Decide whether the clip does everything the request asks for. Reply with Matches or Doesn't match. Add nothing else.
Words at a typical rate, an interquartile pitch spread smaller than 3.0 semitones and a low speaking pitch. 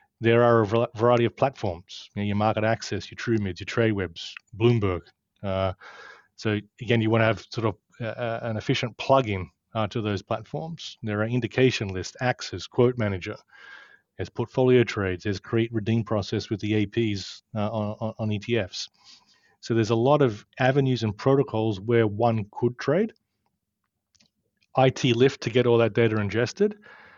Matches